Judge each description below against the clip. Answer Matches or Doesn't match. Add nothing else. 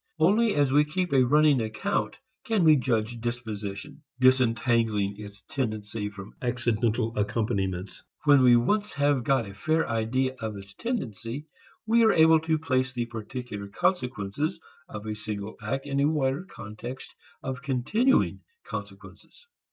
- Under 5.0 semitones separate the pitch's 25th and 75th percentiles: Doesn't match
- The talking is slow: Doesn't match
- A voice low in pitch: Matches